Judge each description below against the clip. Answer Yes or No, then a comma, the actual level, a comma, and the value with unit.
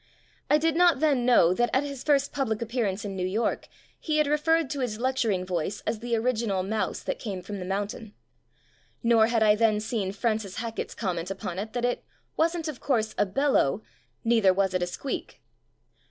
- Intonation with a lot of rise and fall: No, average, 5.0 semitones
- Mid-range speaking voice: No, high, 225 Hz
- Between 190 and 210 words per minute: Yes, average, 200 wpm